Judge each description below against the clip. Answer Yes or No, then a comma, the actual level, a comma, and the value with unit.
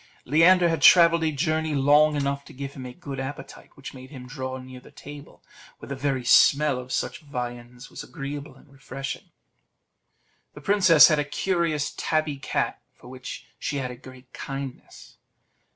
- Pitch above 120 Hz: Yes, medium, 140 Hz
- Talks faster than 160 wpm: Yes, average, 170 wpm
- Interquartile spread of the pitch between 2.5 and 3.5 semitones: Yes, average, 2.8 semitones